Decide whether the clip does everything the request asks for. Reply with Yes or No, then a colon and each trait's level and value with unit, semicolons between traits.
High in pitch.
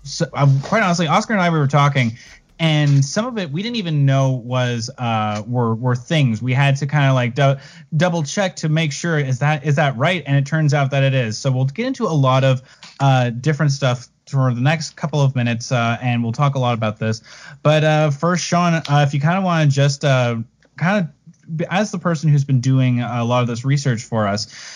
No: medium, 140 Hz